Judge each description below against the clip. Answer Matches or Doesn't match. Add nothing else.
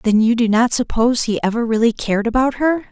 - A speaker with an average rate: Doesn't match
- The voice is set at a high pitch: Matches